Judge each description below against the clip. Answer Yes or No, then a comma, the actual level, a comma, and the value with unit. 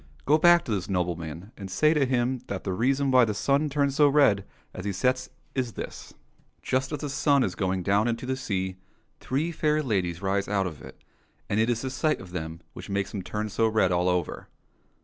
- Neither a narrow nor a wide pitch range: No, wide, 6.3 semitones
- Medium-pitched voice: No, low, 110 Hz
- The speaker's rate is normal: No, fast, 225 wpm